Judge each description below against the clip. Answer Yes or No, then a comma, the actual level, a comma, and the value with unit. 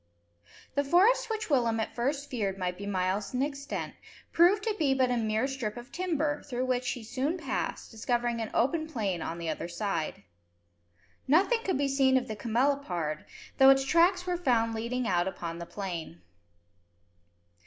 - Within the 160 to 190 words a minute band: Yes, average, 175 wpm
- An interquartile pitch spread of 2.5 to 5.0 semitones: No, wide, 5.6 semitones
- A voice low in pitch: No, very high, 250 Hz